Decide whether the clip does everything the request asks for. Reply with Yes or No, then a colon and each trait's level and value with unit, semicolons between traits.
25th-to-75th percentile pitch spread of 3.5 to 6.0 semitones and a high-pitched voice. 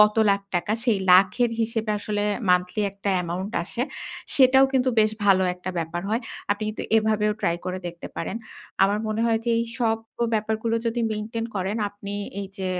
No: average, 2.8 semitones; high, 210 Hz